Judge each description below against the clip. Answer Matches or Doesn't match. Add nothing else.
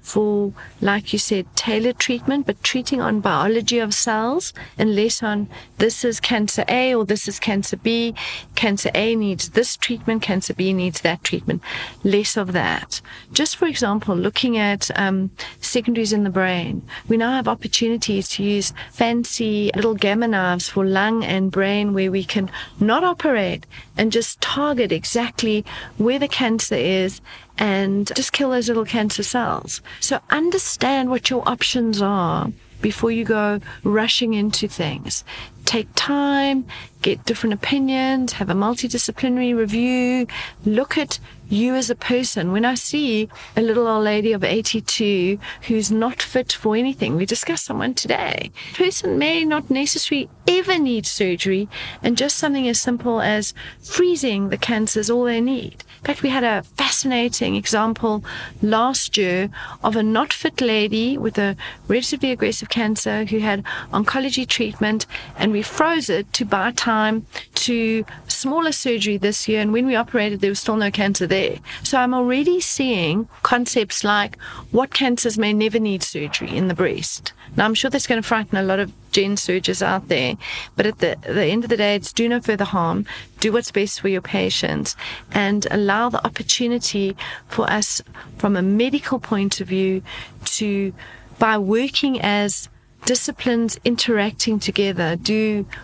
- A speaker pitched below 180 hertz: Doesn't match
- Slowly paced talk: Doesn't match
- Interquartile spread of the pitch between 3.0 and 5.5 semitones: Matches